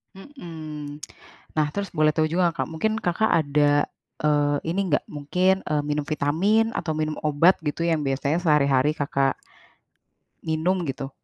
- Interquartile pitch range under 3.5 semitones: Yes, average, 2.9 semitones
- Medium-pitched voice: Yes, medium, 155 Hz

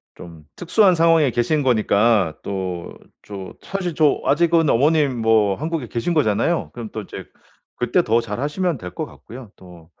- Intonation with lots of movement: Yes, wide, 7.7 semitones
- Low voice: Yes, low, 120 Hz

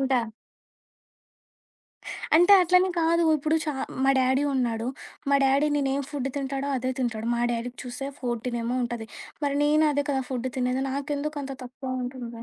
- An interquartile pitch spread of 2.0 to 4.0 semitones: Yes, narrow, 2.6 semitones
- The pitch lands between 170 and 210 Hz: No, very high, 270 Hz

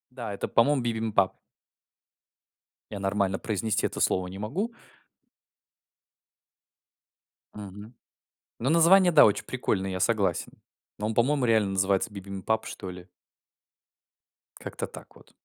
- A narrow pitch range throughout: No, average, 3.5 semitones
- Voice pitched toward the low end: Yes, low, 105 Hz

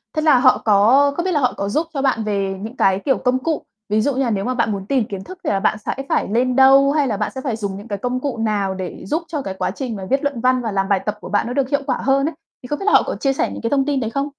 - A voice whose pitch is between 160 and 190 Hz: No, very high, 250 Hz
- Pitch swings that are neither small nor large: Yes, average, 5.0 semitones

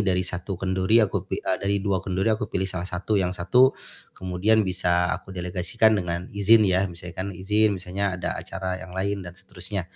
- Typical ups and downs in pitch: No, narrow, 1.8 semitones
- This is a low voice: Yes, very low, 95 Hz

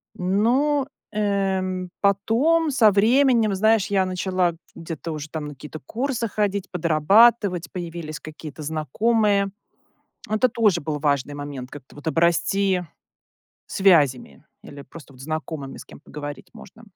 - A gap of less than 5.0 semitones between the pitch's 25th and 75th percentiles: No, wide, 5.6 semitones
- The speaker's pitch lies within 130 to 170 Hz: No, medium, 185 Hz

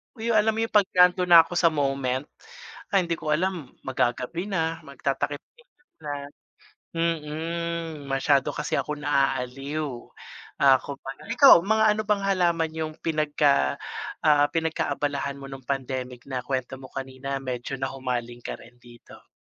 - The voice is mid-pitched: Yes, medium, 145 Hz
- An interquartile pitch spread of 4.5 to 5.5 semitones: No, average, 4.0 semitones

